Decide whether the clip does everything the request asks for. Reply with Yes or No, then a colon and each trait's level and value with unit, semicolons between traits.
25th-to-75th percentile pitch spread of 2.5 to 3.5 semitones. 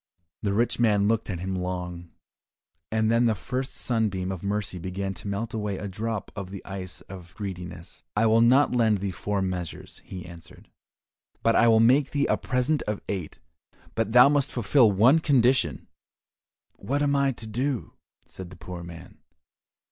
No: average, 4.3 semitones